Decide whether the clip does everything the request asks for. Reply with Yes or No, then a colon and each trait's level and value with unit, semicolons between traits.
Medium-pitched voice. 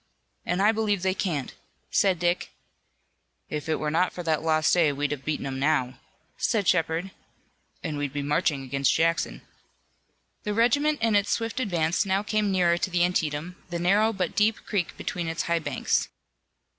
Yes: medium, 175 Hz